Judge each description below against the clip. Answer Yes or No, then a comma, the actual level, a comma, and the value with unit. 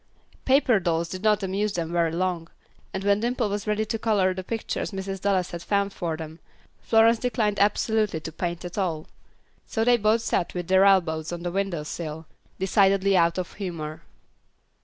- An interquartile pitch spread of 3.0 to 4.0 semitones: Yes, average, 3.6 semitones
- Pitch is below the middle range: No, high, 190 Hz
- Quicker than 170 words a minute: Yes, average, 180 wpm